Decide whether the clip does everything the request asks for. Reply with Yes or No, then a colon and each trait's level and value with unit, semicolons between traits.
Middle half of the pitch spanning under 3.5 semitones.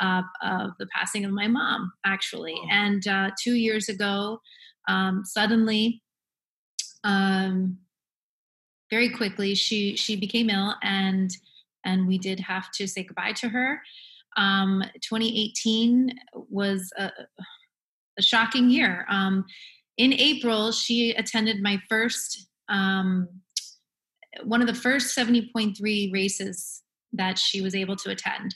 Yes: average, 3.0 semitones